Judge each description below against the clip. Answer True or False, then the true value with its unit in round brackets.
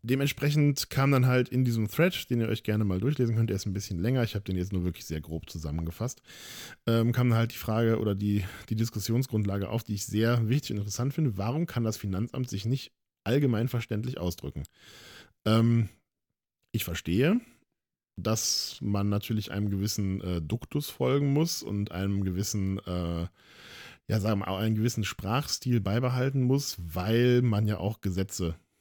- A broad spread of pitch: False (4.0 semitones)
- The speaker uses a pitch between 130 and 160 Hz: False (110 Hz)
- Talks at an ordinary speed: True (175 wpm)